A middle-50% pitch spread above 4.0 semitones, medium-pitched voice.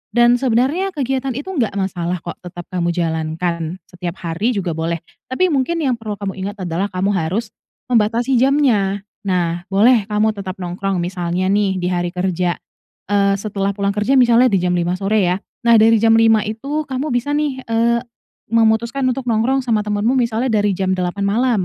No: average, 4.7 semitones; high, 210 Hz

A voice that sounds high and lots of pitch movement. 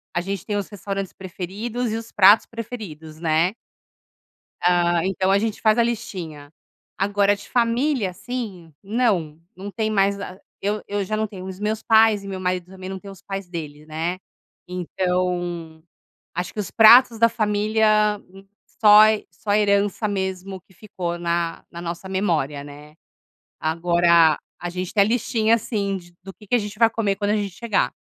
No: high, 195 Hz; average, 3.5 semitones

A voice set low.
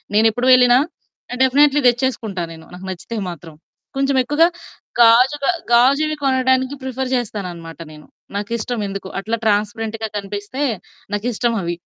No: high, 230 Hz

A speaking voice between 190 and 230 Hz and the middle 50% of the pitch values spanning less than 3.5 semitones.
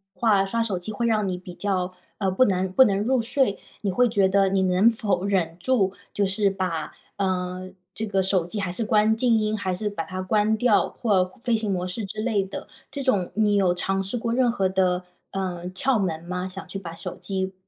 Yes: high, 195 Hz; average, 2.8 semitones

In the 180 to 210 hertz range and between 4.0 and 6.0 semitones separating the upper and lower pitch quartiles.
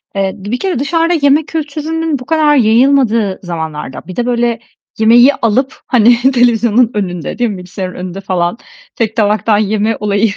No: high, 230 Hz; average, 5.1 semitones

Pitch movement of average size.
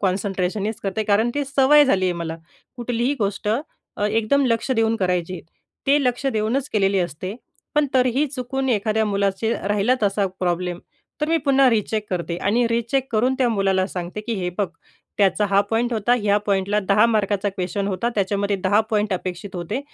Yes: average, 3.7 semitones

